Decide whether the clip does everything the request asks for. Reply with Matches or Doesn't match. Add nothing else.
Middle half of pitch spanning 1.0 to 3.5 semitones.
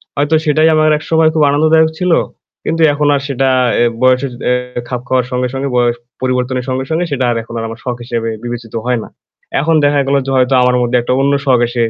Matches